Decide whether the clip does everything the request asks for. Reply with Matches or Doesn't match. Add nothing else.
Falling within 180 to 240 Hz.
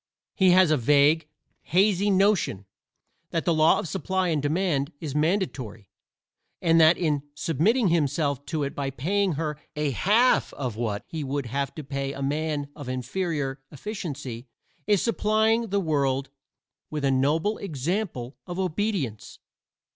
Doesn't match